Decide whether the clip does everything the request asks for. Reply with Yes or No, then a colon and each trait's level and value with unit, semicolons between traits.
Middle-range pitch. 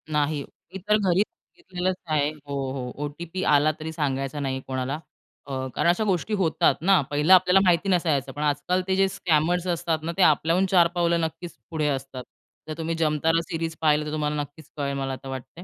Yes: medium, 160 Hz